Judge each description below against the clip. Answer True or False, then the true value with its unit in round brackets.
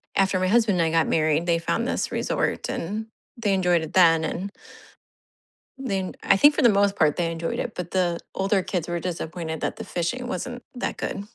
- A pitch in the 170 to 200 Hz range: True (185 Hz)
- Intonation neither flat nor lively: True (3.4 semitones)